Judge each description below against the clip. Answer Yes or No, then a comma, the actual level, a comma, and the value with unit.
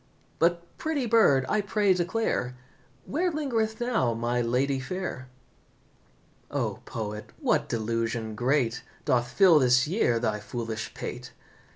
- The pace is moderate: No, slow, 120 wpm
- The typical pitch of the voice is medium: No, low, 130 Hz